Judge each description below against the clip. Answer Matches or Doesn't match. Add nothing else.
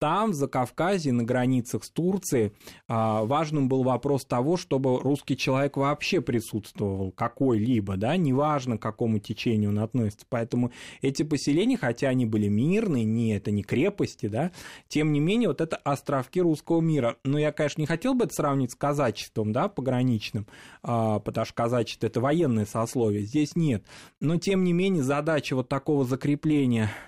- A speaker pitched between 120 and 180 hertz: Matches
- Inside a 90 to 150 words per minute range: Doesn't match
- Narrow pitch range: Doesn't match